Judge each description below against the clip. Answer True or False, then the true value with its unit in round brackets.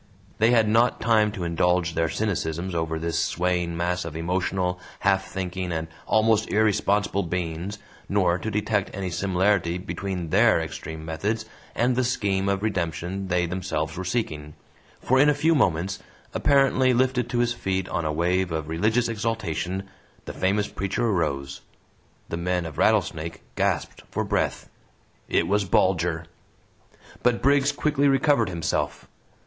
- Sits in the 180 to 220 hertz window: False (95 Hz)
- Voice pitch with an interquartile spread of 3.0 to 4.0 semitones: False (4.5 semitones)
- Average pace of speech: True (150 wpm)